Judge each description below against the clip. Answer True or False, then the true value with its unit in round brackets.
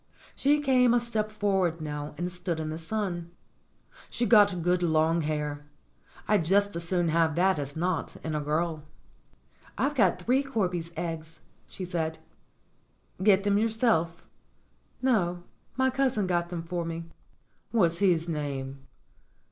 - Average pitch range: True (4.2 semitones)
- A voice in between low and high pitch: True (175 Hz)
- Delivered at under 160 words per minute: True (150 wpm)